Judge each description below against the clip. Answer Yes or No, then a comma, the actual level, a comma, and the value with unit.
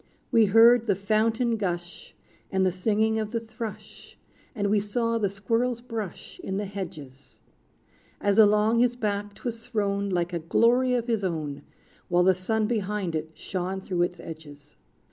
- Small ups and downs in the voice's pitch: No, average, 3.7 semitones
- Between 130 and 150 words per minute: No, average, 165 wpm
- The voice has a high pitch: Yes, high, 205 Hz